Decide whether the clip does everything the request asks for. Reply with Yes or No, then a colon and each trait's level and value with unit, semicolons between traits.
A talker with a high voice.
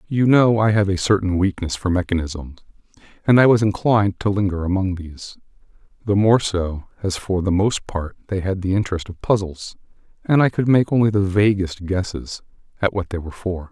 No: very low, 95 Hz